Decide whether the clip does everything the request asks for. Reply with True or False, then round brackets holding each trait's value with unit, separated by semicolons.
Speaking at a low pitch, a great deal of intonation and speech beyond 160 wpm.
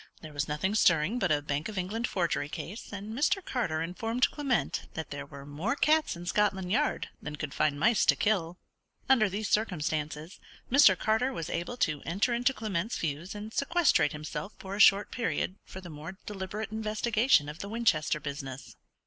False (190 Hz; 6.4 semitones; 185 wpm)